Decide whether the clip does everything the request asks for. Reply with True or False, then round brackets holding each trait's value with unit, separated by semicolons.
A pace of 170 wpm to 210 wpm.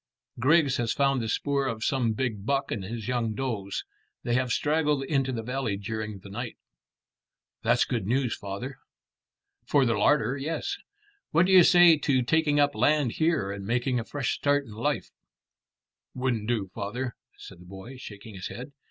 True (175 wpm)